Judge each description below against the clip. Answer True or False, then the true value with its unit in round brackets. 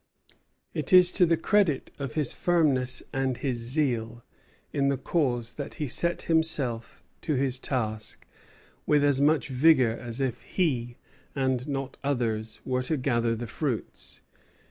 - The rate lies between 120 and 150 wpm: True (145 wpm)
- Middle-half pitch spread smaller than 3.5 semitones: False (3.9 semitones)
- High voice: False (135 Hz)